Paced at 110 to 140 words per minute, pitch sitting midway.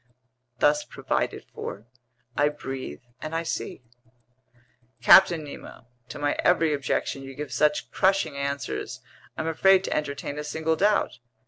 Yes: slow, 135 wpm; medium, 150 Hz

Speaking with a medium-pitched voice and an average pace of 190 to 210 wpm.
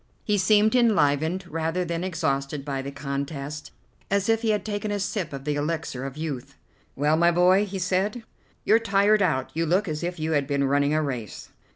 Yes: medium, 165 Hz; average, 200 wpm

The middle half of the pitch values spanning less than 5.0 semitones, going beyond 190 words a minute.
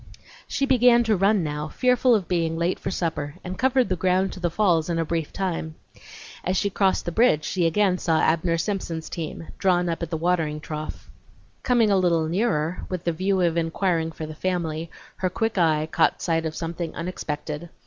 Yes: average, 3.0 semitones; average, 200 wpm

